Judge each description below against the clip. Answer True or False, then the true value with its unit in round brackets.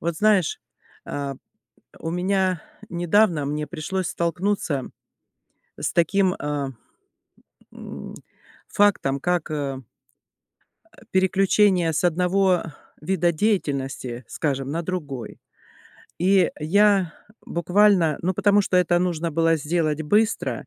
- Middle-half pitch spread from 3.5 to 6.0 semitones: True (3.9 semitones)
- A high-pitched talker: False (170 Hz)